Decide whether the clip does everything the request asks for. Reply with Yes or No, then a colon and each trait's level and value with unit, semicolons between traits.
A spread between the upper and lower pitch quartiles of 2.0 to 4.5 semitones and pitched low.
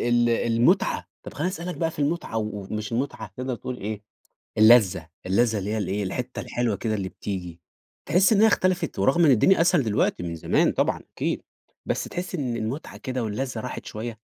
No: average, 5.2 semitones; low, 120 Hz